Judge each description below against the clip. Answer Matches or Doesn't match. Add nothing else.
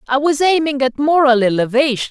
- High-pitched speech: Matches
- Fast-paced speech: Doesn't match